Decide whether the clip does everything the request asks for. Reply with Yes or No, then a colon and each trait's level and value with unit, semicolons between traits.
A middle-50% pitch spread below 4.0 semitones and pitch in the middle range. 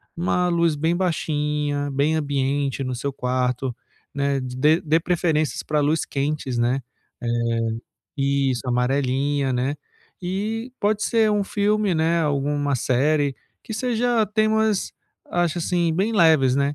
No: average, 4.6 semitones; medium, 150 Hz